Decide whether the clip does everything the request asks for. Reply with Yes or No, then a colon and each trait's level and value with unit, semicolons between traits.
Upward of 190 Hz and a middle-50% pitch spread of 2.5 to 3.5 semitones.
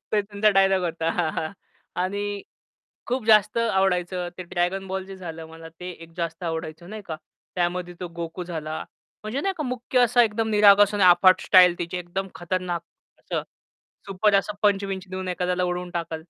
No: medium, 185 Hz; average, 2.8 semitones